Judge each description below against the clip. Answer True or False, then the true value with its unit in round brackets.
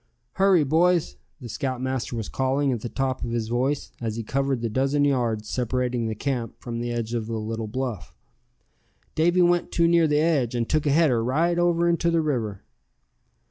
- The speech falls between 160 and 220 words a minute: True (190 wpm)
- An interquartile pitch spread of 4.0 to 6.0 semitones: True (5.0 semitones)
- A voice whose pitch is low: True (130 Hz)